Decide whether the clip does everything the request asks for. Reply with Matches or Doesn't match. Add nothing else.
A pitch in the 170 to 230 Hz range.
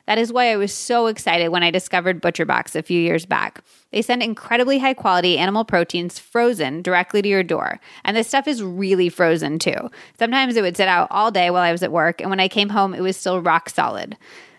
Matches